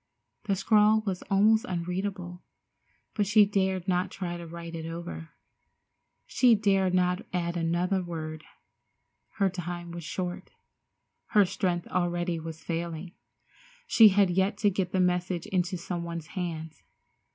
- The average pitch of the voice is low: No, medium, 180 Hz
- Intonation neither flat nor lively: No, narrow, 2.2 semitones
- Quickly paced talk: No, average, 140 wpm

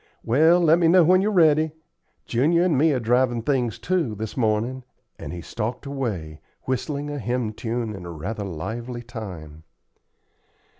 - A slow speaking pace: No, average, 155 wpm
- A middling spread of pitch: No, wide, 5.7 semitones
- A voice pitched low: Yes, low, 120 Hz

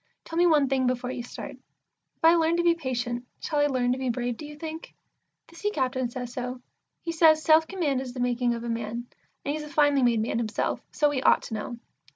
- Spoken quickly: Yes, fast, 240 wpm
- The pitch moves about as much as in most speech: Yes, average, 4.2 semitones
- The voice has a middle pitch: No, very high, 260 Hz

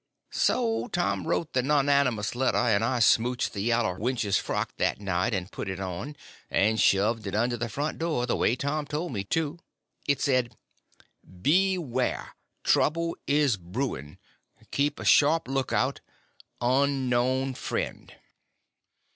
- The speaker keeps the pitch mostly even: No, average, 4.8 semitones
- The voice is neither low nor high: No, low, 125 Hz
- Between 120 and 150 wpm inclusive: Yes, average, 140 wpm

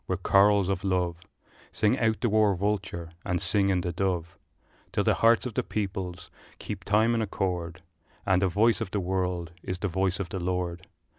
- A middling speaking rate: Yes, average, 195 wpm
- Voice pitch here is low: Yes, very low, 95 Hz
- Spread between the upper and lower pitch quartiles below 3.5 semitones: Yes, narrow, 2.5 semitones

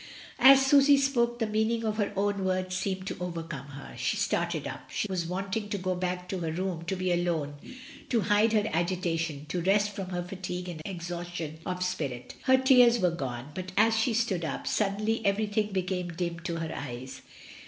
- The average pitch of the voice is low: No, medium, 185 Hz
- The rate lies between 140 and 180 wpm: No, average, 195 wpm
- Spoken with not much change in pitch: No, average, 3.7 semitones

